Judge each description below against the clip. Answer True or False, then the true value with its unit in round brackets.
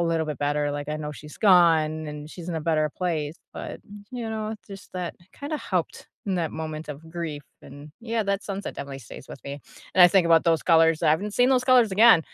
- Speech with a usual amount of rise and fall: True (4.6 semitones)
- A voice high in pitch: False (165 Hz)